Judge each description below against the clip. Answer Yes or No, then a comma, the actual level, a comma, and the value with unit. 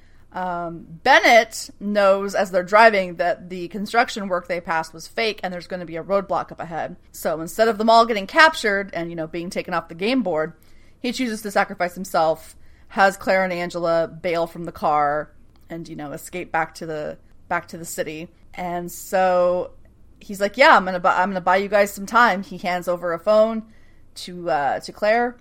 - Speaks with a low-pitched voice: No, medium, 180 Hz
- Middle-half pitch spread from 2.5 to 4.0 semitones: Yes, average, 3.5 semitones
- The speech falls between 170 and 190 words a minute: No, fast, 205 wpm